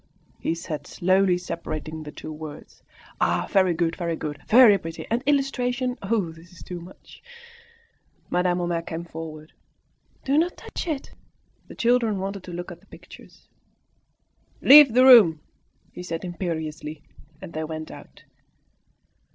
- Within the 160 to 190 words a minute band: No, average, 150 wpm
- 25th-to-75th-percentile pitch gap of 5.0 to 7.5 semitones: Yes, wide, 5.5 semitones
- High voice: No, medium, 175 Hz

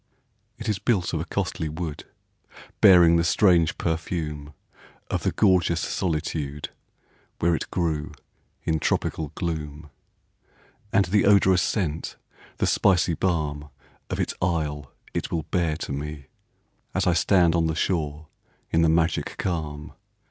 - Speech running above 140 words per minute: No, slow, 135 wpm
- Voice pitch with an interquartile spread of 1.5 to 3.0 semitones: Yes, average, 2.7 semitones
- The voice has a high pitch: No, very low, 80 Hz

